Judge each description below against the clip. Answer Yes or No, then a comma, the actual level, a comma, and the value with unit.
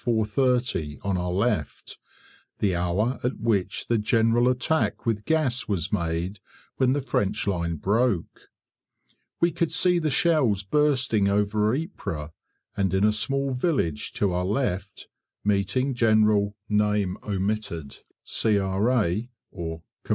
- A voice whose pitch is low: Yes, low, 105 Hz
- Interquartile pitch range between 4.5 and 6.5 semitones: Yes, average, 4.8 semitones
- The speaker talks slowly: Yes, slow, 115 wpm